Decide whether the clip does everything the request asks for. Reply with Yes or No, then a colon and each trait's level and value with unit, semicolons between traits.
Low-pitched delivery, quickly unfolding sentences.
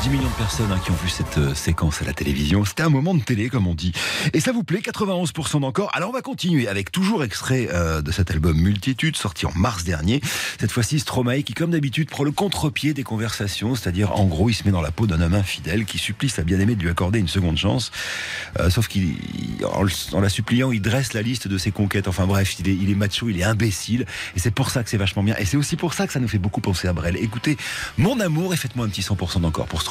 Yes: low, 105 Hz; fast, 265 wpm